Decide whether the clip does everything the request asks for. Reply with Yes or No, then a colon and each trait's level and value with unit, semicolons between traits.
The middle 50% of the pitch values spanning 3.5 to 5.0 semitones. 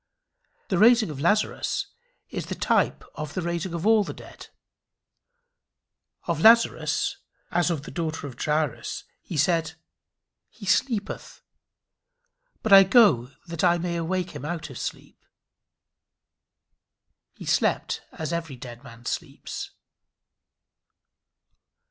Yes: average, 4.0 semitones